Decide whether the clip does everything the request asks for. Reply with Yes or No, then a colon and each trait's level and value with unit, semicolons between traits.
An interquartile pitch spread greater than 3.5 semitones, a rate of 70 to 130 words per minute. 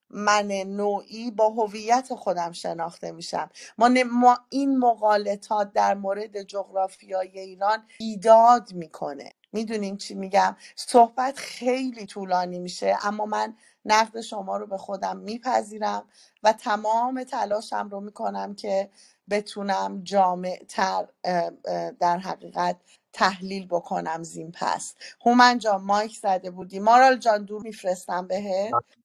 No: average, 2.9 semitones; average, 115 wpm